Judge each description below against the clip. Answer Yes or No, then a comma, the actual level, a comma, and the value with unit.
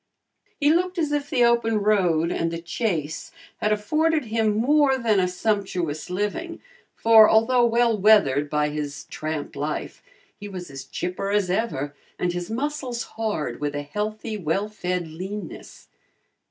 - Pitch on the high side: Yes, high, 210 Hz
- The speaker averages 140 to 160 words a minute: Yes, average, 155 wpm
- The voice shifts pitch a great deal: Yes, wide, 5.8 semitones